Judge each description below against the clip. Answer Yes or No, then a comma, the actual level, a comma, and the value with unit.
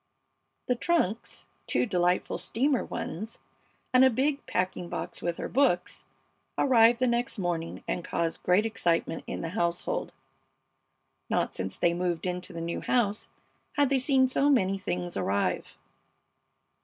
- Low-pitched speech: No, high, 195 Hz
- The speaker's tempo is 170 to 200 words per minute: No, average, 145 wpm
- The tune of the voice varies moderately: No, wide, 6.5 semitones